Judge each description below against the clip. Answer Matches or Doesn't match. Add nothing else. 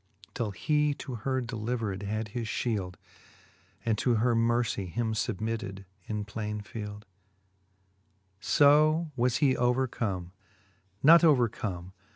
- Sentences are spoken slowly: Matches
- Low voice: Matches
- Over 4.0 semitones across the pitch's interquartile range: Doesn't match